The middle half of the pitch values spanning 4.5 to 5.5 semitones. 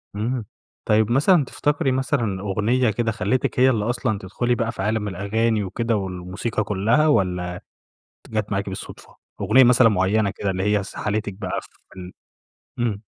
No: average, 3.5 semitones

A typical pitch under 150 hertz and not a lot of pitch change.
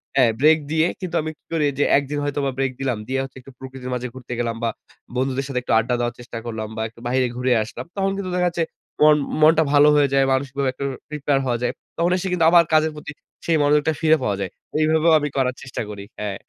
No: low, 135 Hz; average, 3.9 semitones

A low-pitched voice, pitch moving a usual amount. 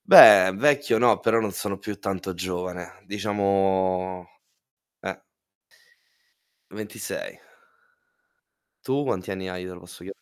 No: very low, 95 Hz; narrow, 2.0 semitones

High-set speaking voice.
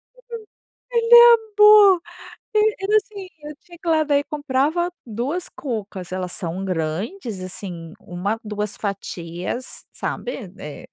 Yes: very high, 260 Hz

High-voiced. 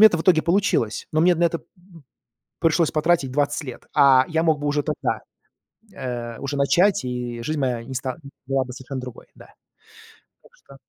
No: medium, 145 Hz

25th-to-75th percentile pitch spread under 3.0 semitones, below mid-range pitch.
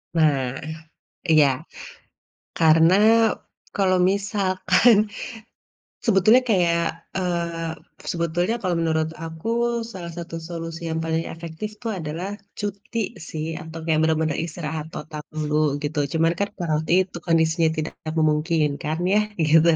No: narrow, 2.5 semitones; medium, 165 Hz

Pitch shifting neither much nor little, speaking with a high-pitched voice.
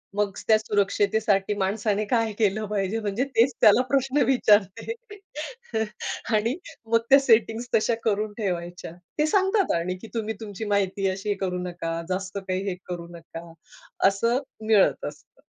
Yes: average, 3.0 semitones; high, 210 Hz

